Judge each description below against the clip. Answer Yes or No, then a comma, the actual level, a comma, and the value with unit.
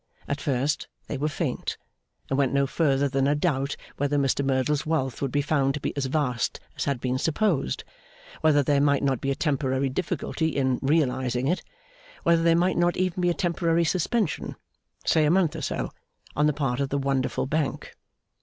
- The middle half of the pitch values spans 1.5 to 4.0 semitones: Yes, average, 3.0 semitones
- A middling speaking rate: Yes, average, 190 wpm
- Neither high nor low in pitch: Yes, medium, 145 Hz